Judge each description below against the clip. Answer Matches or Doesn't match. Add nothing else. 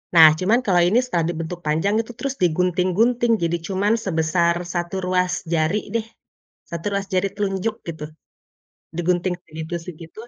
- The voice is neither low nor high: Matches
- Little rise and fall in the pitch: Doesn't match